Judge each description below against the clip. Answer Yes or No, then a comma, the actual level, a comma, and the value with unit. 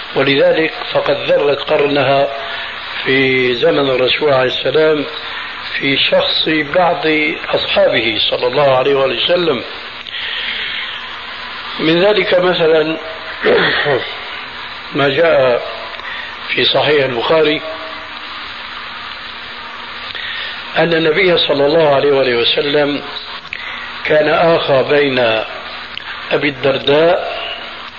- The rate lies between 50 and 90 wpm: Yes, average, 75 wpm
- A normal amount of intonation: Yes, average, 3.2 semitones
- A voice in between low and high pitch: Yes, medium, 155 Hz